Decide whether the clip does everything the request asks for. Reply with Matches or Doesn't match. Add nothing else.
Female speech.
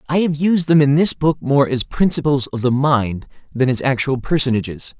Doesn't match